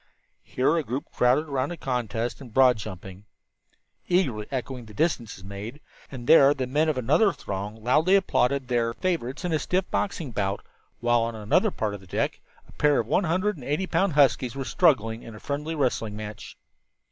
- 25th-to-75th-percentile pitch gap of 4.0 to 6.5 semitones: Yes, wide, 5.4 semitones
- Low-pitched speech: Yes, low, 130 Hz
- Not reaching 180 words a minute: No, average, 190 wpm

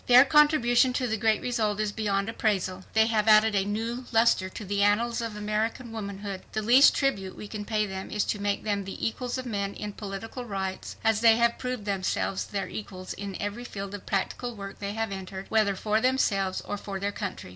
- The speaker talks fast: Yes, fast, 210 wpm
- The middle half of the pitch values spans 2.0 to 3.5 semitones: Yes, narrow, 2.5 semitones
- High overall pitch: Yes, high, 210 Hz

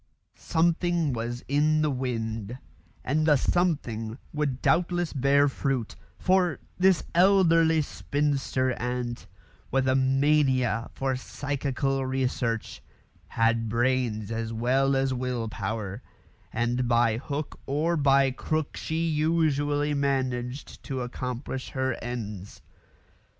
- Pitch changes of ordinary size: Yes, average, 3.6 semitones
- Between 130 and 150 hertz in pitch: Yes, low, 135 Hz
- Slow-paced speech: Yes, slow, 110 wpm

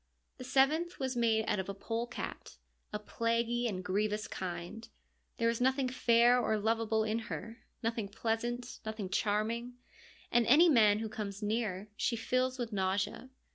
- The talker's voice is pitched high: Yes, high, 225 Hz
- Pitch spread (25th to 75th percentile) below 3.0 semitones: Yes, narrow, 2.4 semitones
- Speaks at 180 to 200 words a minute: No, average, 160 wpm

